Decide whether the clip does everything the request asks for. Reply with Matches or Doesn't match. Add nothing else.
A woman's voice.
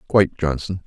Doesn't match